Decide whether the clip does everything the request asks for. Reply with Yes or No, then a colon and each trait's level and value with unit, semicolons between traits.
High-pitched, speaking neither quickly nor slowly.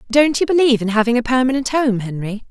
No: high, 245 Hz; fast, 215 wpm